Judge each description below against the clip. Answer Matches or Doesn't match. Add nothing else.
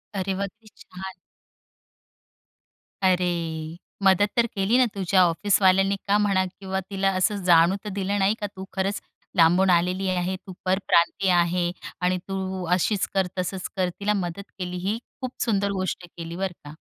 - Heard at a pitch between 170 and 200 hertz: Matches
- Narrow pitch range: Matches